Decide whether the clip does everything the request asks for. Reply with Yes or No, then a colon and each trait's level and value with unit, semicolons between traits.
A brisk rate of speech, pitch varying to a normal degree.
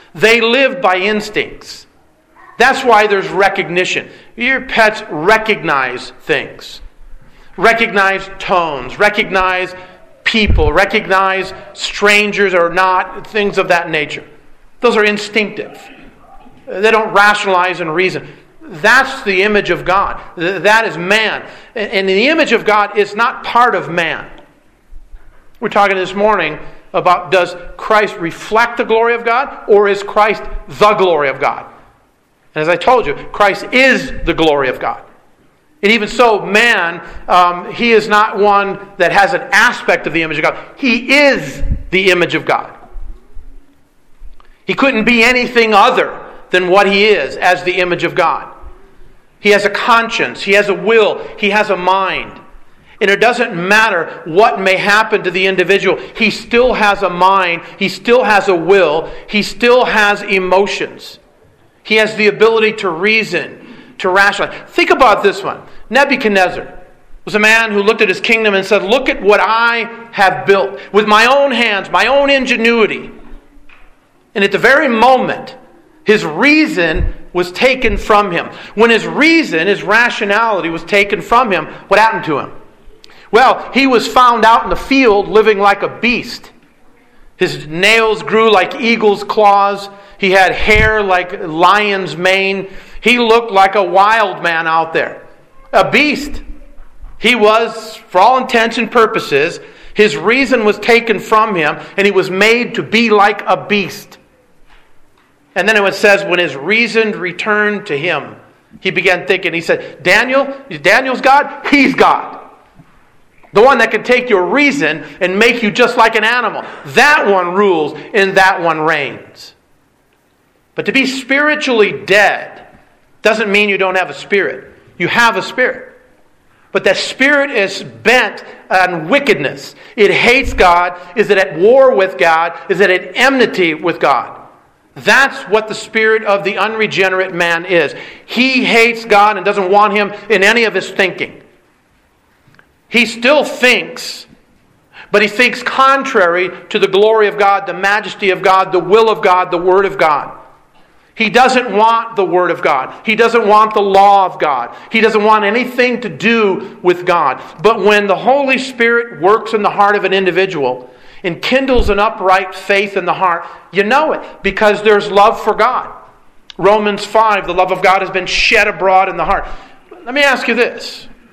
No: average, 160 wpm; average, 3.4 semitones